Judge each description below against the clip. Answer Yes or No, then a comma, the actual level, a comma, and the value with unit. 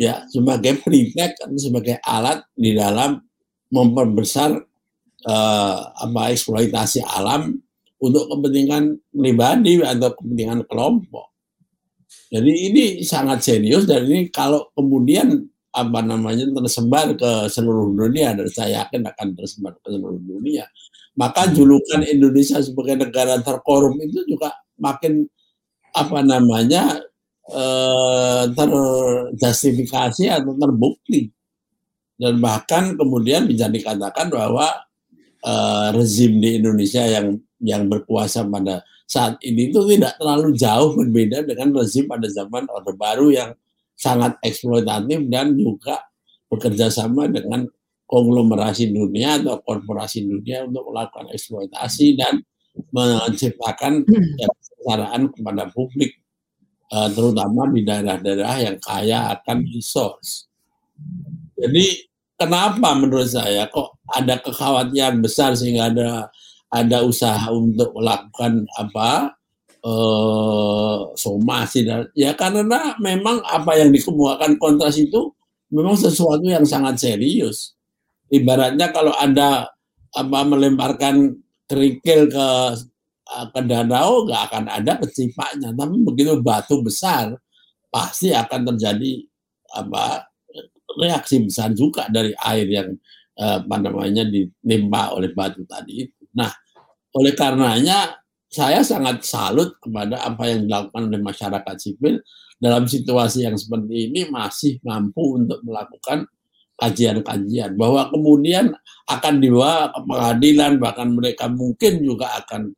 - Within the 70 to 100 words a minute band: No, average, 110 wpm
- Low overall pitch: Yes, low, 125 Hz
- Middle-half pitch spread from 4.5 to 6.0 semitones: Yes, average, 4.8 semitones